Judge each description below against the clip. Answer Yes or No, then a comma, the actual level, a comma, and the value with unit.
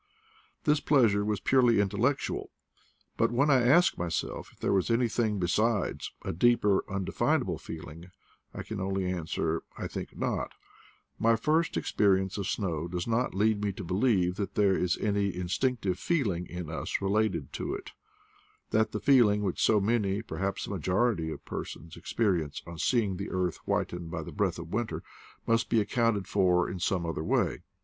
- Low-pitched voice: Yes, low, 100 Hz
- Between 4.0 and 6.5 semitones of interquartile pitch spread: Yes, average, 4.3 semitones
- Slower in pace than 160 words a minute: No, average, 170 wpm